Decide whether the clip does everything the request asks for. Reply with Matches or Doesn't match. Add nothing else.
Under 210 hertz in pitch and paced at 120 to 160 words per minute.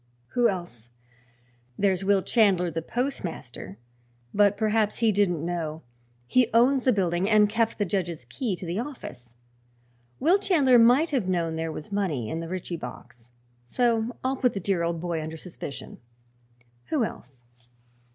Matches